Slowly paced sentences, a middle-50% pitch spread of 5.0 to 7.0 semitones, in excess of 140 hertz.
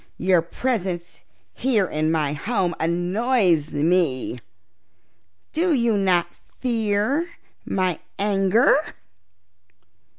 Yes: slow, 80 wpm; average, 5.3 semitones; high, 190 Hz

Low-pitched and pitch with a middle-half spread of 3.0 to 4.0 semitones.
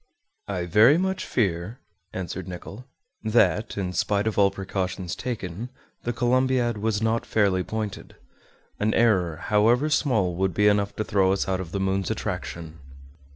Yes: low, 105 Hz; average, 3.4 semitones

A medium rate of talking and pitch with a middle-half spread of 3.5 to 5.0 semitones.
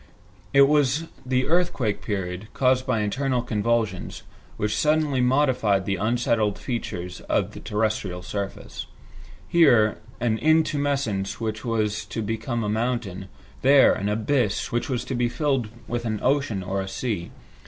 Yes: average, 145 wpm; average, 4.1 semitones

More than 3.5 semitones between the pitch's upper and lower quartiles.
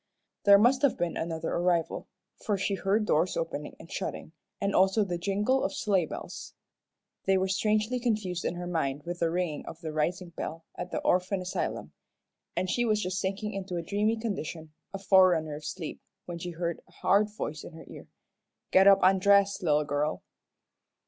No: average, 3.2 semitones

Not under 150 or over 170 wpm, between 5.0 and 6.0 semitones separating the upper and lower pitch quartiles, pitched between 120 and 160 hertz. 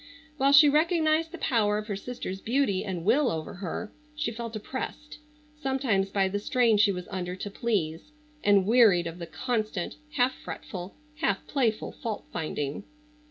No: average, 160 wpm; wide, 5.5 semitones; high, 215 Hz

